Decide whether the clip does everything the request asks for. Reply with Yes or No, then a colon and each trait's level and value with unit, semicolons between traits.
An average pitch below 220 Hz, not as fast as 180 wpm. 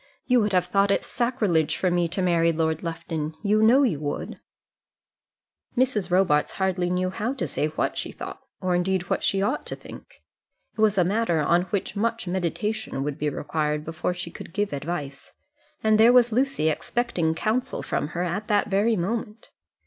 No: medium, 185 Hz; average, 185 wpm